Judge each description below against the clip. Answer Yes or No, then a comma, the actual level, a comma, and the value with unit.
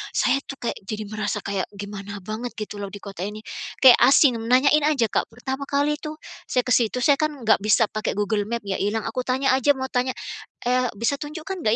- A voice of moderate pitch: No, high, 235 Hz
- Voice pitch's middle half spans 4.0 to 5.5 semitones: Yes, average, 4.4 semitones